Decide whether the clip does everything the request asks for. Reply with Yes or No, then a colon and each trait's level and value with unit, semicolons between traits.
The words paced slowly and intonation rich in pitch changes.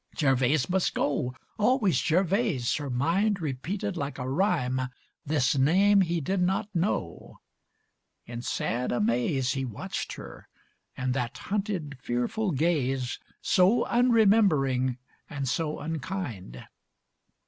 Yes: slow, 115 wpm; wide, 7.0 semitones